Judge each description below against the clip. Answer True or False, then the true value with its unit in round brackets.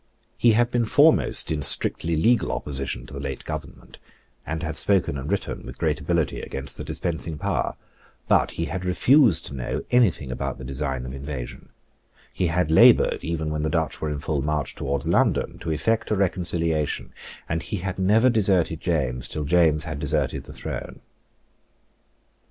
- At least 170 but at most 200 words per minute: True (175 wpm)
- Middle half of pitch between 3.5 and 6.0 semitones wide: True (4.6 semitones)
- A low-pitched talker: True (80 Hz)